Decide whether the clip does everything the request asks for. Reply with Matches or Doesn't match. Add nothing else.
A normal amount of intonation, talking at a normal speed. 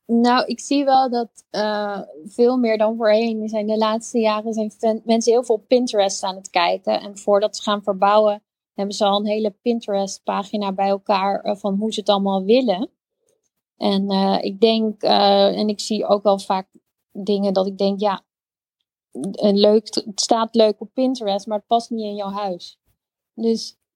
Doesn't match